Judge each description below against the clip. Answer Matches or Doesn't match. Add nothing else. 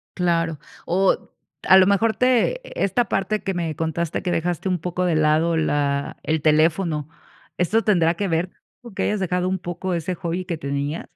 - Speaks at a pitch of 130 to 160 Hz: Doesn't match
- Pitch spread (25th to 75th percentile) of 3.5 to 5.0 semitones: Doesn't match